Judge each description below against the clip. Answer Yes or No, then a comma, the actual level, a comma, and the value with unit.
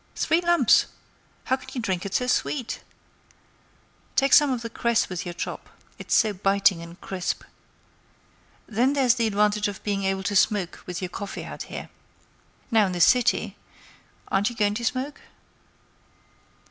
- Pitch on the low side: No, high, 210 Hz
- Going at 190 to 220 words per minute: No, average, 160 wpm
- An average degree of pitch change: Yes, average, 4.5 semitones